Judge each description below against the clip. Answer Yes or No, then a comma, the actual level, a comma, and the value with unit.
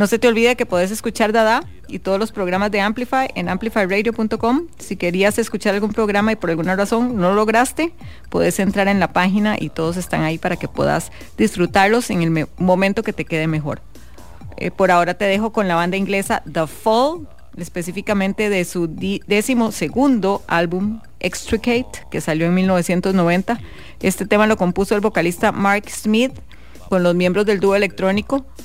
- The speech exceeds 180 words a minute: No, average, 175 wpm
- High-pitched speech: Yes, high, 200 Hz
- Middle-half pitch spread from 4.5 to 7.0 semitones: No, average, 3.7 semitones